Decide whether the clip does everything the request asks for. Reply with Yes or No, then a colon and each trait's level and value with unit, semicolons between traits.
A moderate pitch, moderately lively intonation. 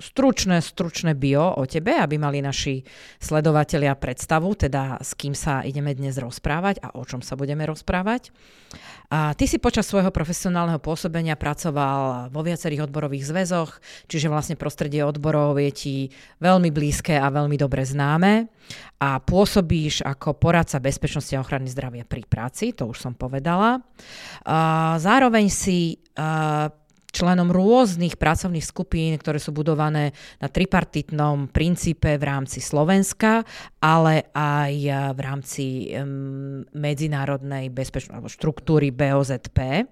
Yes: medium, 150 Hz; average, 3.6 semitones